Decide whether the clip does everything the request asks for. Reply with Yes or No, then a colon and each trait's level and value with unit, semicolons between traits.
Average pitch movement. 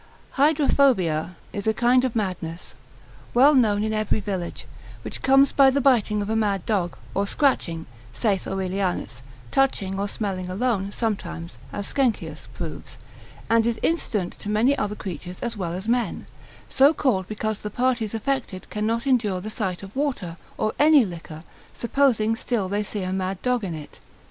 Yes: average, 4.7 semitones